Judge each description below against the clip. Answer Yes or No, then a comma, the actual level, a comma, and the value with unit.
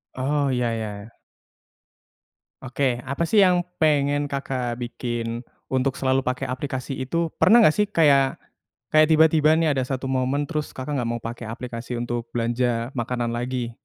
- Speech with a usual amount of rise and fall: Yes, average, 3.3 semitones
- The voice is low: Yes, low, 130 Hz